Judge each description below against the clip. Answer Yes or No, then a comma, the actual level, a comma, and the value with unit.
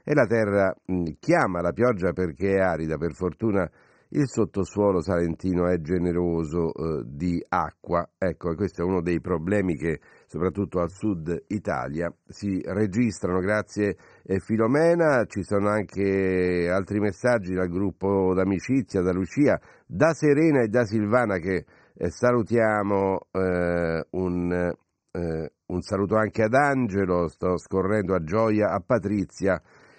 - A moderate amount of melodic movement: Yes, average, 3.2 semitones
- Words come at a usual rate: Yes, average, 135 wpm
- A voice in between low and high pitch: No, very low, 95 Hz